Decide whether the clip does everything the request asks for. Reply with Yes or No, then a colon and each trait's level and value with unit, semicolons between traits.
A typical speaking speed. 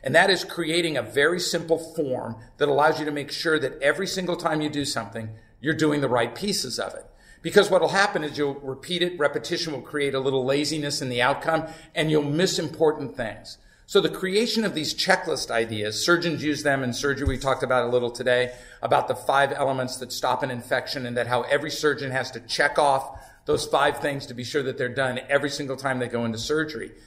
No: fast, 225 wpm